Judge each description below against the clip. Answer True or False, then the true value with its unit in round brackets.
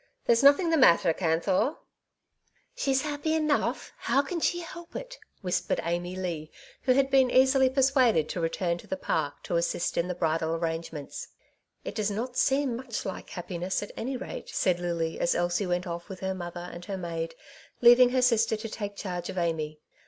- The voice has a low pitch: False (190 Hz)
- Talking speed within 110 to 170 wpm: False (195 wpm)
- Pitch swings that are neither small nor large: False (7.3 semitones)